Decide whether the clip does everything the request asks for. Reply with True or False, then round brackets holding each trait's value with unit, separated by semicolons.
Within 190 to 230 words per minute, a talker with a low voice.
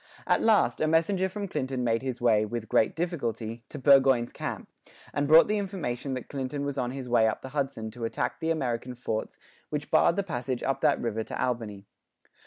True (200 wpm; 130 Hz)